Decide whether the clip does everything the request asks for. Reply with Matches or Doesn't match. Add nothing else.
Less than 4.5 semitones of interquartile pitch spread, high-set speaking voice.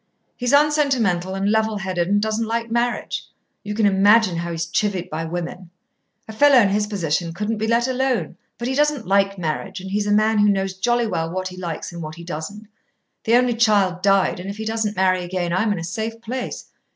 Matches